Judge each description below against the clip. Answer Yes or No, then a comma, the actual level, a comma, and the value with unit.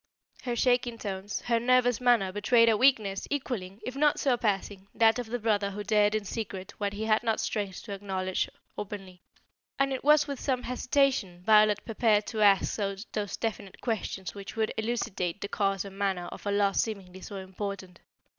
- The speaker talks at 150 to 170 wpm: No, average, 180 wpm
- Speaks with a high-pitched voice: Yes, high, 210 Hz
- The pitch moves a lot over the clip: No, average, 3.4 semitones